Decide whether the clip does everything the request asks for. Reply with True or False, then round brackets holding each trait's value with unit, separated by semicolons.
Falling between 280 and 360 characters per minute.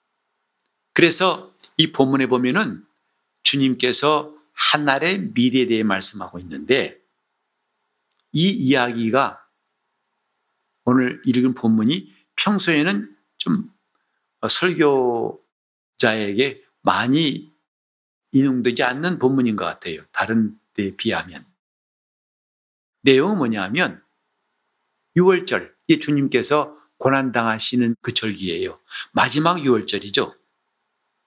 False (205 characters per minute)